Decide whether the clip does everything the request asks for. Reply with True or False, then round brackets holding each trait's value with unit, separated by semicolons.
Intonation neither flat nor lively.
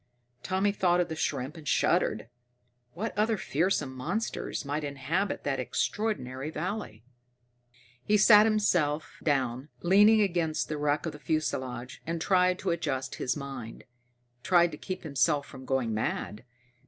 False (5.8 semitones)